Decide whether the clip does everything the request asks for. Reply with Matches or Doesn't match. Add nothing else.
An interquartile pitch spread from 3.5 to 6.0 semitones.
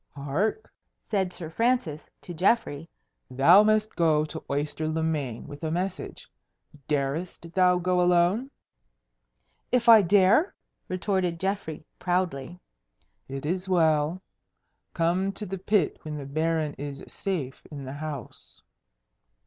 Matches